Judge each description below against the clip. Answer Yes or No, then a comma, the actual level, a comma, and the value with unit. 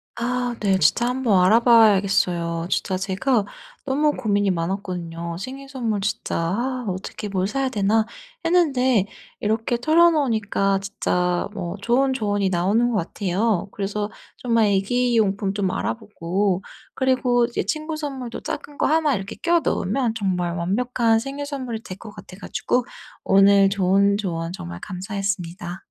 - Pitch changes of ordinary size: Yes, average, 4.6 semitones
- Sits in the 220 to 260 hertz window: No, high, 210 Hz